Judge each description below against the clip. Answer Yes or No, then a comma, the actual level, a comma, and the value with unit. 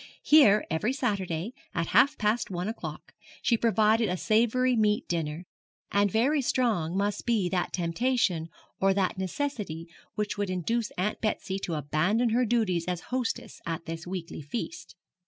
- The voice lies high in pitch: Yes, high, 205 Hz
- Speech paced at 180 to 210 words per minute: No, average, 155 wpm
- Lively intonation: No, average, 4.9 semitones